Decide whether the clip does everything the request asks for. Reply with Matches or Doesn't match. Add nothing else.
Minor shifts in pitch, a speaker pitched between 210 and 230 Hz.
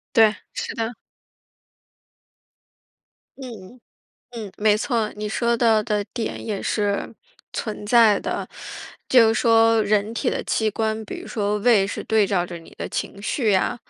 Matches